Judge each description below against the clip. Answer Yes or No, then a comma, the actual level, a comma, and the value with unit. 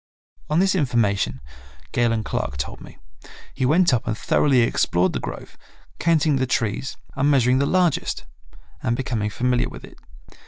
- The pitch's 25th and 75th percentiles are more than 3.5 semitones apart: Yes, average, 4.4 semitones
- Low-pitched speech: Yes, low, 125 Hz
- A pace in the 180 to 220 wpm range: No, average, 155 wpm